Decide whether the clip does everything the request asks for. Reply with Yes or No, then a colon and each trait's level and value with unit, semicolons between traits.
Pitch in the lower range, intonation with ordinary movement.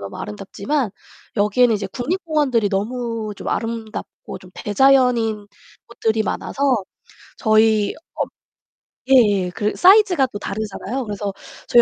No: high, 225 Hz; average, 3.7 semitones